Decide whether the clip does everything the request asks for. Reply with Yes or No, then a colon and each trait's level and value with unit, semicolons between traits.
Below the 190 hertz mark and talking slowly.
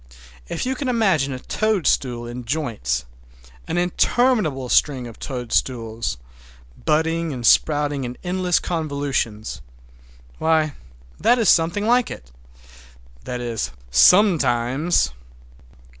Yes: medium, 140 Hz; slow, 100 wpm